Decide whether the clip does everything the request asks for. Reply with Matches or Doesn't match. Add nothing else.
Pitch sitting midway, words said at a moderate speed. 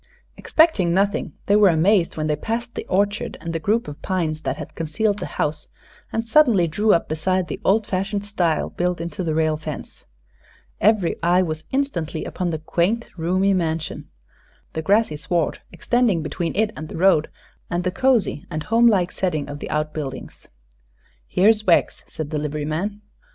Matches